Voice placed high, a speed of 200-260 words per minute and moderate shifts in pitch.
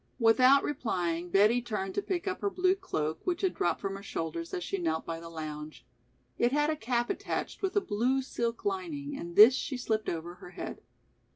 No: high, 225 Hz; fast, 205 wpm; wide, 8.8 semitones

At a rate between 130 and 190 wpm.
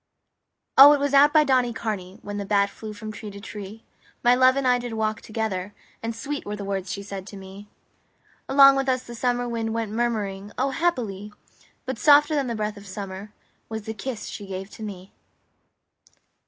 No: average, 200 wpm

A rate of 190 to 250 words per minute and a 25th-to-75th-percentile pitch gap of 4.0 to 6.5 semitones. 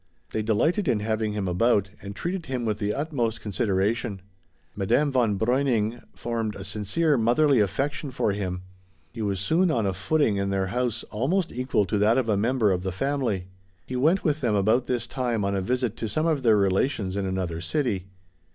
Yes: average, 195 wpm; average, 4.6 semitones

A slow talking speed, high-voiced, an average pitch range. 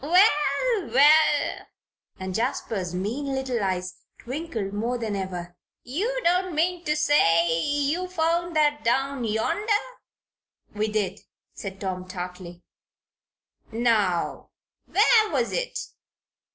No: slow, 110 wpm; very high, 250 Hz; wide, 8.4 semitones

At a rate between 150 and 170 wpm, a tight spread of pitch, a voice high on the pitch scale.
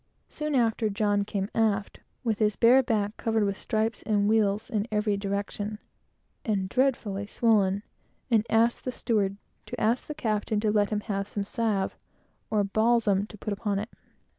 Yes: average, 165 wpm; narrow, 1.9 semitones; high, 210 Hz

